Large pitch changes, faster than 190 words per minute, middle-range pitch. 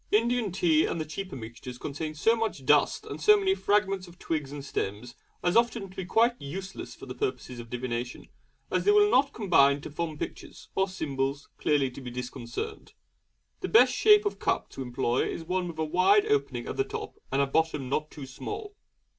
Yes: wide, 9.0 semitones; fast, 205 wpm; medium, 165 Hz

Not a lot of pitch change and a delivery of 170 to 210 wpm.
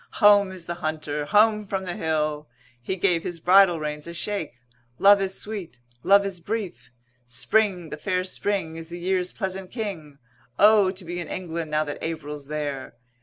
No: average, 4.2 semitones; average, 175 wpm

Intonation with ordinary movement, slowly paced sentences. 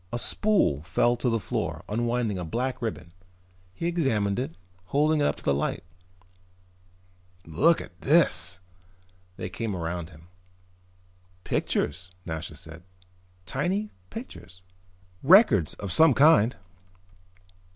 No: wide, 8.7 semitones; slow, 120 wpm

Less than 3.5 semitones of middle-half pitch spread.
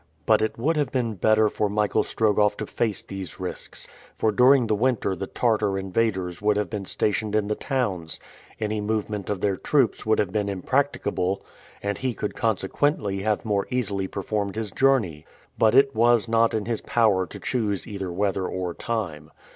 Yes: average, 2.8 semitones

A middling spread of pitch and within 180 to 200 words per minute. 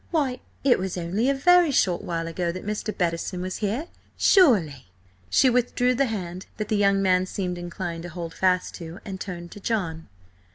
Yes: average, 5.0 semitones; average, 190 wpm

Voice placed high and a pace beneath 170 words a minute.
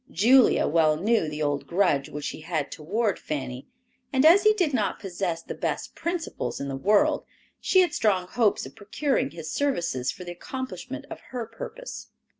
No: high, 195 Hz; average, 180 wpm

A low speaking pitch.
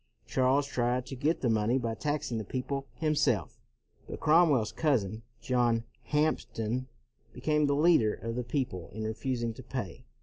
Yes: low, 125 Hz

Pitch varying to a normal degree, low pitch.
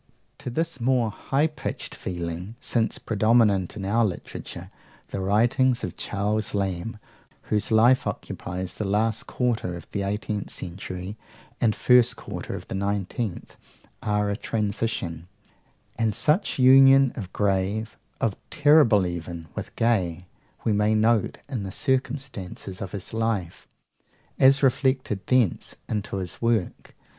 Yes: average, 3.9 semitones; low, 105 Hz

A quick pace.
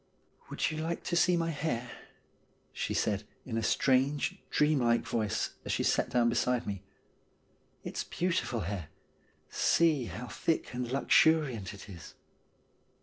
No: average, 145 wpm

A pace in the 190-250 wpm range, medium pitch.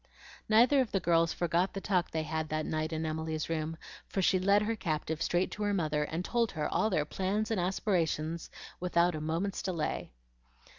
Yes: average, 195 wpm; medium, 170 Hz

